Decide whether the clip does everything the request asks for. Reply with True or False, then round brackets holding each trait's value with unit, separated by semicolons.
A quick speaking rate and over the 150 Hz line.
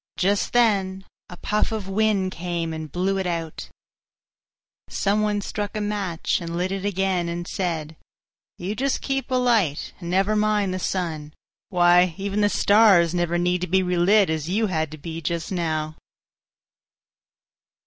False (160 wpm; 185 Hz)